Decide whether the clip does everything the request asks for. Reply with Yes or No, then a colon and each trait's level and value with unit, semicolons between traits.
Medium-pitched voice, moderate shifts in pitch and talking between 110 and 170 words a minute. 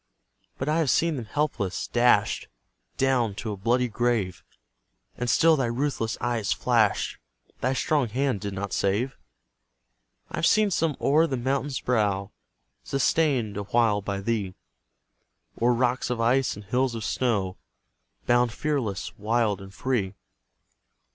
No: low, 120 Hz; average, 4.3 semitones; average, 140 wpm